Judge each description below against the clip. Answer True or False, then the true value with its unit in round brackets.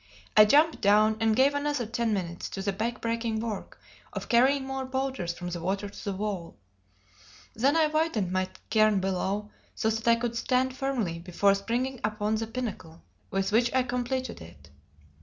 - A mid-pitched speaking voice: False (220 Hz)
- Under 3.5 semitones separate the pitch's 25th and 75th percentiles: False (4.6 semitones)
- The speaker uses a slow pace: False (175 wpm)